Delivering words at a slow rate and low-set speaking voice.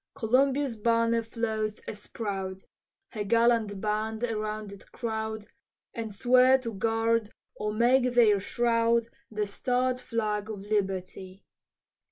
No: slow, 120 wpm; high, 220 Hz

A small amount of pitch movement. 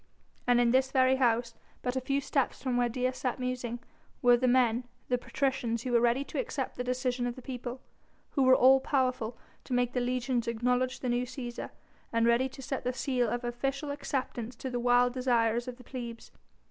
Yes: narrow, 1.3 semitones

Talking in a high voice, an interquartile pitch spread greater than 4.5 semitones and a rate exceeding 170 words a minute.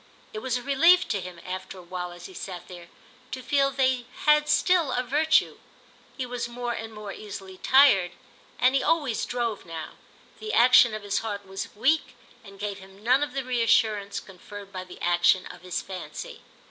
Yes: high, 215 Hz; wide, 5.5 semitones; average, 190 wpm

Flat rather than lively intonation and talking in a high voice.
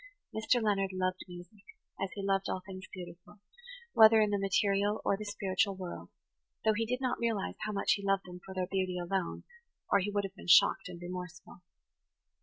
Yes: narrow, 2.0 semitones; high, 195 Hz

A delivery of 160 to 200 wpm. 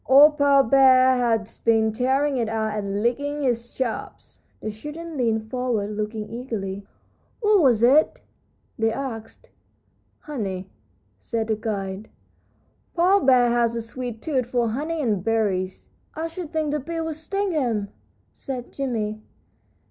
No: average, 140 wpm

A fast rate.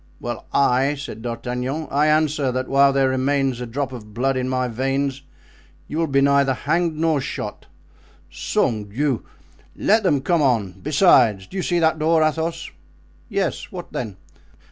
No: average, 160 wpm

